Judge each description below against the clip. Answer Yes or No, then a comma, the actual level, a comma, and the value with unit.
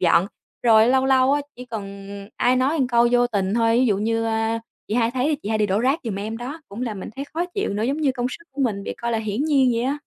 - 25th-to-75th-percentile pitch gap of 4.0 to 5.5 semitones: No, average, 3.3 semitones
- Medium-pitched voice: No, high, 235 Hz